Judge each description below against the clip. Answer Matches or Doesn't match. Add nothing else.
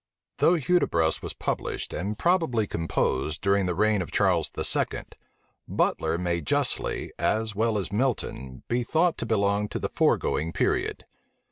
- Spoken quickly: Doesn't match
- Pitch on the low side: Matches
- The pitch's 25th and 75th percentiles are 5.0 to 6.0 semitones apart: Matches